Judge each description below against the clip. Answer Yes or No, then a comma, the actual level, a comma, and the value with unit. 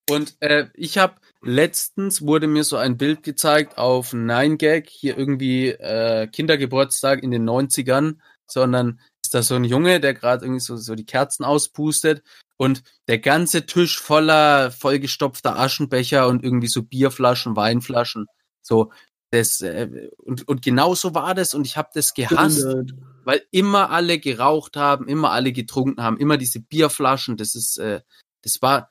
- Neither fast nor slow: Yes, average, 160 wpm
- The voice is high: No, low, 135 Hz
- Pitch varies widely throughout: No, average, 3.3 semitones